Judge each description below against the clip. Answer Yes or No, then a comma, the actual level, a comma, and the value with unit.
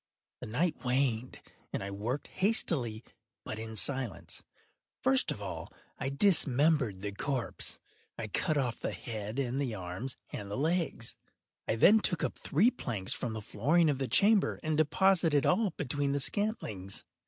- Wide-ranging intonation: Yes, wide, 6.3 semitones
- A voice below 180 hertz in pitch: Yes, low, 135 Hz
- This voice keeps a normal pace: Yes, average, 160 wpm